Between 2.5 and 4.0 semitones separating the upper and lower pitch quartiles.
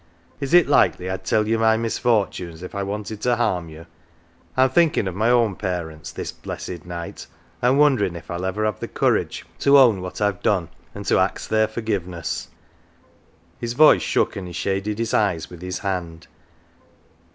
No: average, 4.4 semitones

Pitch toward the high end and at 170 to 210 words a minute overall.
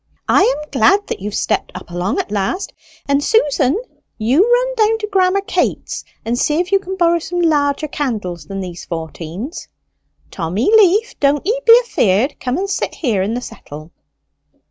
Yes: very high, 290 Hz; average, 175 wpm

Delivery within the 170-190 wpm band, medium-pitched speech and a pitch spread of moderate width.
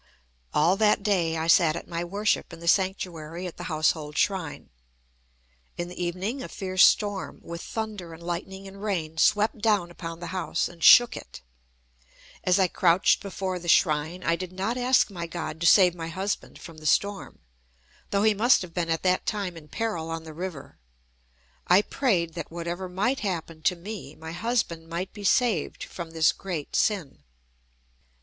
Yes: average, 180 wpm; medium, 180 Hz; average, 3.2 semitones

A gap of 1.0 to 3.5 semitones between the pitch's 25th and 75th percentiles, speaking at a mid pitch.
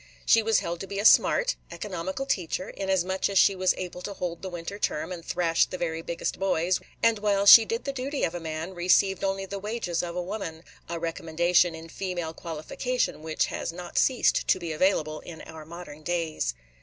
Yes: average, 3.0 semitones; medium, 180 Hz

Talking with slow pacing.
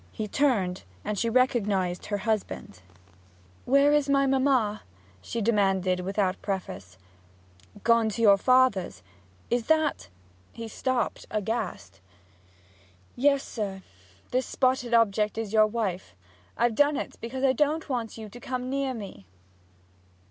Yes: slow, 130 wpm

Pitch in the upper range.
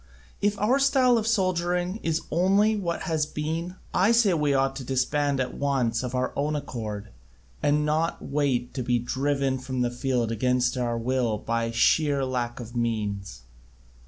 No: medium, 140 Hz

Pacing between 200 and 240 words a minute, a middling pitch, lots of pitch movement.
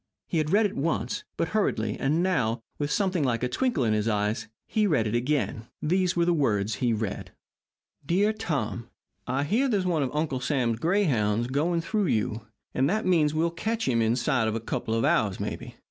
Yes: fast, 205 wpm; medium, 145 Hz; wide, 7.5 semitones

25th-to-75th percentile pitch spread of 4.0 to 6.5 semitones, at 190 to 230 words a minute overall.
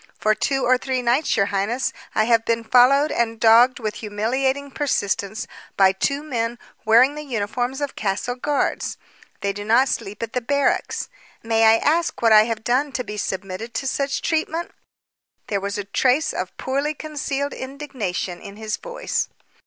No: average, 4.5 semitones; average, 170 wpm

